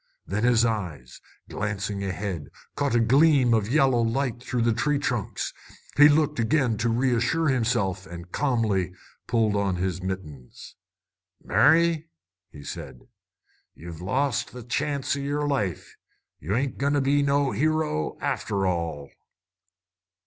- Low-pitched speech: Yes, low, 115 Hz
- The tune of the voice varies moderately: No, wide, 6.5 semitones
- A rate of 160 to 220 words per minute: No, slow, 135 wpm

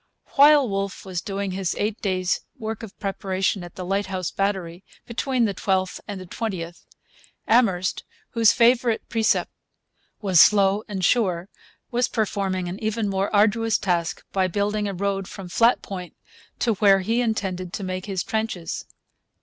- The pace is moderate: Yes, average, 155 wpm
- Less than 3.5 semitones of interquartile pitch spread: Yes, average, 2.8 semitones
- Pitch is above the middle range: Yes, high, 195 Hz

